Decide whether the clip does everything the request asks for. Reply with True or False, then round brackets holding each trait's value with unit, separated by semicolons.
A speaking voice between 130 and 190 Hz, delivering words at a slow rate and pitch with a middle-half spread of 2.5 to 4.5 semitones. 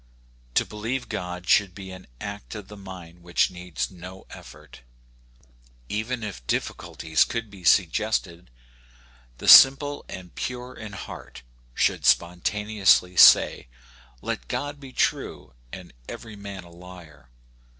False (95 Hz; 130 wpm; 3.7 semitones)